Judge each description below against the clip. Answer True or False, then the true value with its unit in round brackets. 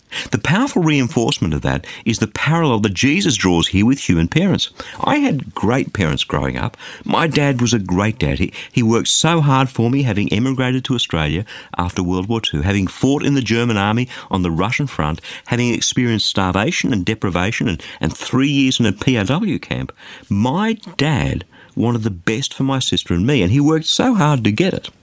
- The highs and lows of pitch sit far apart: True (5.8 semitones)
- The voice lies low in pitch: True (120 Hz)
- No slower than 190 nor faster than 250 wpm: True (195 wpm)